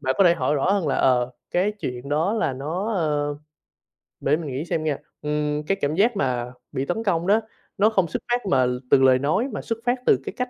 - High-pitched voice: No, medium, 155 Hz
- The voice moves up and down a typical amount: No, wide, 6.2 semitones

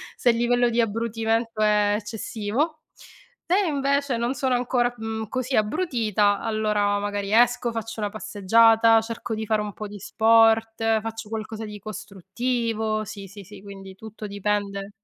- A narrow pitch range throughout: Yes, narrow, 2.0 semitones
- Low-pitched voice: No, high, 220 Hz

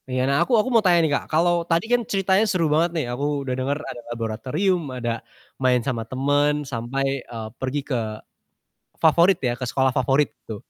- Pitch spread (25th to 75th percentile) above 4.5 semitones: Yes, average, 5.1 semitones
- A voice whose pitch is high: No, medium, 140 Hz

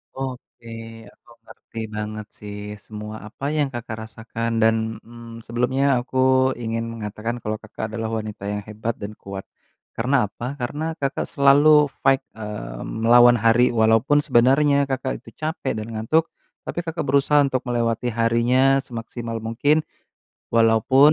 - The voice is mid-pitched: No, low, 115 Hz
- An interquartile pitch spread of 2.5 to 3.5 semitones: Yes, average, 3.0 semitones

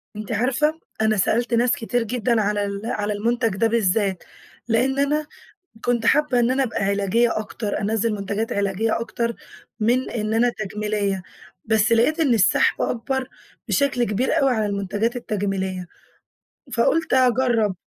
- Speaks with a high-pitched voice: Yes, high, 225 Hz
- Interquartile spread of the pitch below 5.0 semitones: Yes, average, 3.2 semitones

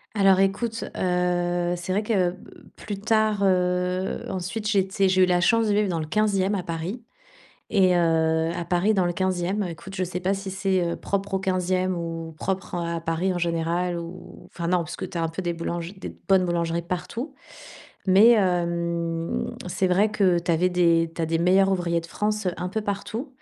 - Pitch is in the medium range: Yes, medium, 180 Hz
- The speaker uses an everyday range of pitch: No, narrow, 2.3 semitones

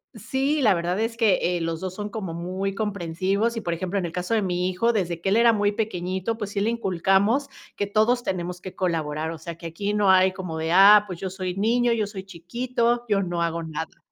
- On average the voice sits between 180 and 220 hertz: Yes, high, 190 Hz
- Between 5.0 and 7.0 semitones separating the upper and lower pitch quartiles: No, average, 3.7 semitones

